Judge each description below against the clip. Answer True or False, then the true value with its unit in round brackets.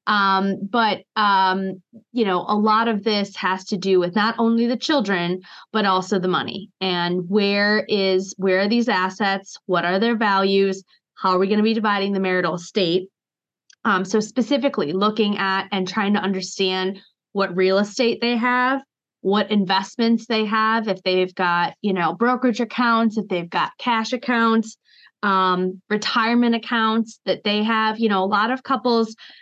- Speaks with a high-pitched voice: True (205 Hz)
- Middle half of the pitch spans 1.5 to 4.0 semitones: True (3.1 semitones)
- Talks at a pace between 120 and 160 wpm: False (170 wpm)